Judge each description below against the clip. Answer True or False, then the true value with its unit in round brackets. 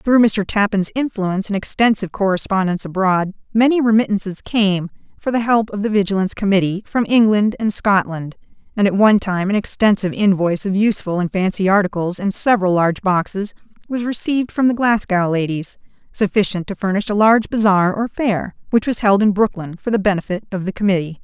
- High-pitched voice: True (200 Hz)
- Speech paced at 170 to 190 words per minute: True (180 wpm)